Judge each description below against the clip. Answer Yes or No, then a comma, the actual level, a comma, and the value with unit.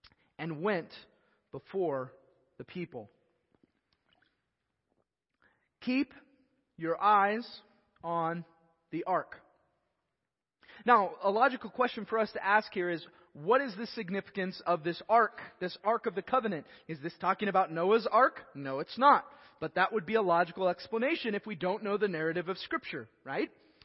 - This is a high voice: Yes, high, 205 Hz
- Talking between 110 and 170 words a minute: Yes, average, 145 wpm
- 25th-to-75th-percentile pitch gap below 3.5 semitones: No, average, 4.7 semitones